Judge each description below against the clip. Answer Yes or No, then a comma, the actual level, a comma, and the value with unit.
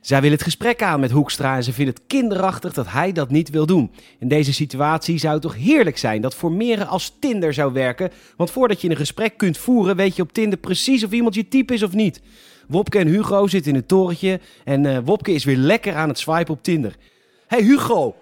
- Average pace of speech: No, fast, 235 wpm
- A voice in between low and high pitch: Yes, medium, 170 Hz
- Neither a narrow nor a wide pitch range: No, wide, 6.0 semitones